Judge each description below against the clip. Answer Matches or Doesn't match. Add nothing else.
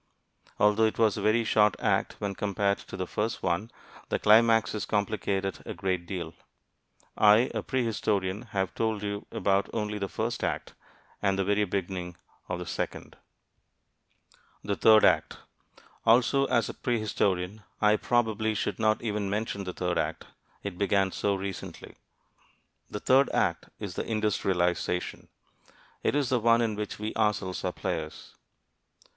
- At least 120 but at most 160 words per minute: Matches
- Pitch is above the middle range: Doesn't match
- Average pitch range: Doesn't match